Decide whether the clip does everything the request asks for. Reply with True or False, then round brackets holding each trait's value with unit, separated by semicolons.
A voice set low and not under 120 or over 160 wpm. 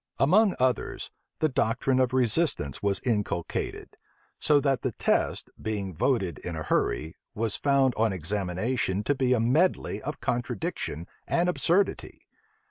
True (120 Hz; 135 wpm)